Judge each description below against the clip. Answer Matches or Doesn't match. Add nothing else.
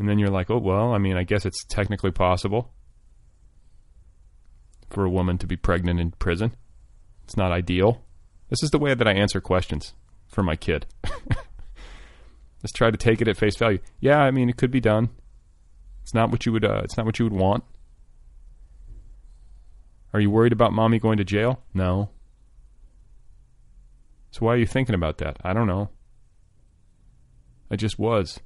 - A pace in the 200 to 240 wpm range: Doesn't match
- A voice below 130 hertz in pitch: Matches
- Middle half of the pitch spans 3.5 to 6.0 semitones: Matches